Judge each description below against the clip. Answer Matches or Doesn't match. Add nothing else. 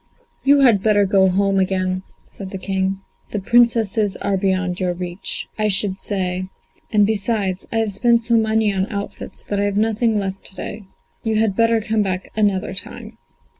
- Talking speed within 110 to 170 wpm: Doesn't match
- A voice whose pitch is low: Doesn't match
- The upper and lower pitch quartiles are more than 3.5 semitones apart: Doesn't match